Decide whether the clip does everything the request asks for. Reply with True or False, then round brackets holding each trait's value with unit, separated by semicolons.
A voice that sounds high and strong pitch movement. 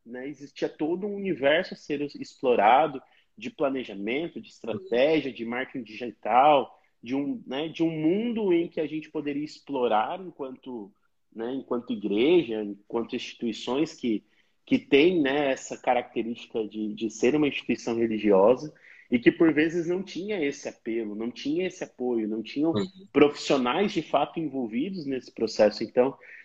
False (140 Hz; 5.8 semitones)